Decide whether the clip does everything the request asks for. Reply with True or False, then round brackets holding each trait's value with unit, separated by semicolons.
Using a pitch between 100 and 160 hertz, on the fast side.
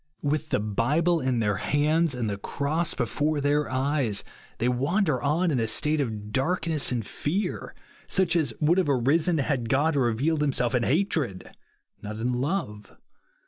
False (140 Hz; 165 wpm)